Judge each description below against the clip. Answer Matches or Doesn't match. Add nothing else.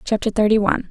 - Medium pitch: Doesn't match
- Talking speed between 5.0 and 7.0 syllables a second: Doesn't match